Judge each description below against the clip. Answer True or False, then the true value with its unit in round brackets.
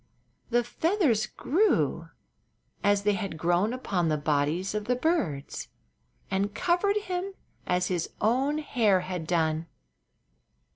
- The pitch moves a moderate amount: False (8.4 semitones)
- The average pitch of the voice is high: True (205 Hz)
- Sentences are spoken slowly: True (125 wpm)